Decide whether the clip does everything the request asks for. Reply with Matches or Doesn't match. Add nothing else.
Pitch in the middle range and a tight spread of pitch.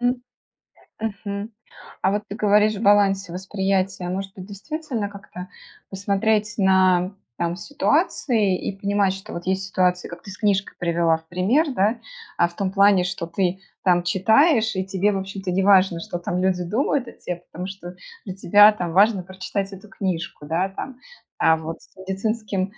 Doesn't match